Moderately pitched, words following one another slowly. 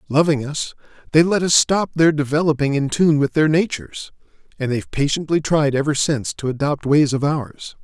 No: medium, 150 Hz; average, 185 wpm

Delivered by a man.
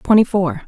No: female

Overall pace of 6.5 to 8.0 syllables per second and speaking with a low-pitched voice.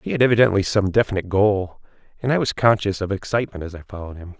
Yes: 7.2 syllables/s; low, 100 Hz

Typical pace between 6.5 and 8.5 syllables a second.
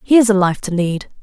No: 5.9 syllables/s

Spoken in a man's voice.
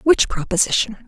No: female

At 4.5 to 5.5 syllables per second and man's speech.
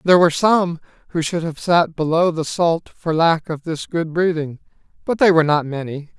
Yes: 5.1 syllables/s; male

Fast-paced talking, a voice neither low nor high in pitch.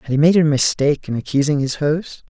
Yes: fast, 235 wpm; medium, 150 Hz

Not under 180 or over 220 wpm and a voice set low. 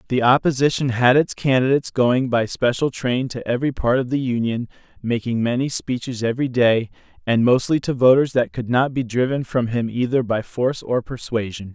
Yes: average, 185 wpm; low, 125 Hz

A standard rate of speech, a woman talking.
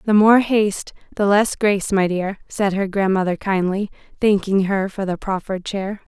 Yes: average, 175 wpm; female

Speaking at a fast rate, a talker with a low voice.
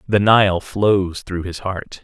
No: average, 175 wpm; very low, 95 Hz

